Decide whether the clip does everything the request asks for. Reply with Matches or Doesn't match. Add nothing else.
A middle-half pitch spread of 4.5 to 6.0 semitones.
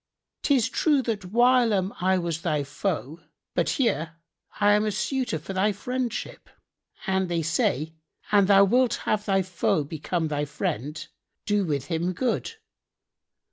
Matches